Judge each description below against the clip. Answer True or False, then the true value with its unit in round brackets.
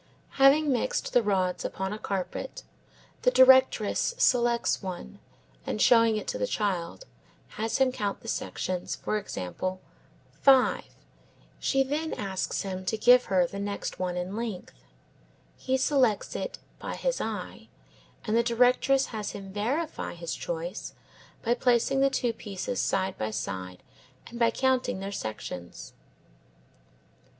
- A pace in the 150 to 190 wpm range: False (140 wpm)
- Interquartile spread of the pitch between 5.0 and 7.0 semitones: True (5.4 semitones)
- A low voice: False (215 Hz)